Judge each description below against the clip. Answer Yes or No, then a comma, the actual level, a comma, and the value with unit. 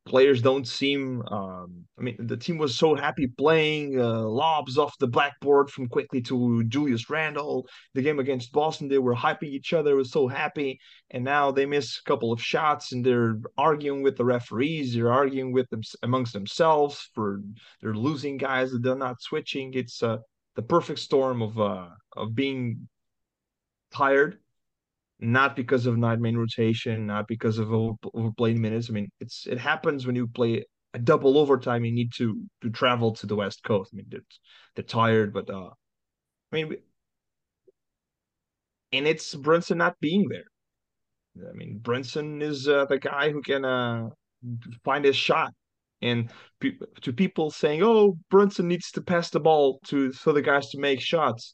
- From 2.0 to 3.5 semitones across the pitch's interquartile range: No, average, 4.0 semitones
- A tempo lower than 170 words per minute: No, average, 175 wpm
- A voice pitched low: Yes, low, 130 Hz